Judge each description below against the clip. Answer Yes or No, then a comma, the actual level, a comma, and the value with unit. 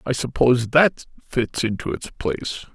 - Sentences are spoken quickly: No, average, 155 wpm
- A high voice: No, low, 125 Hz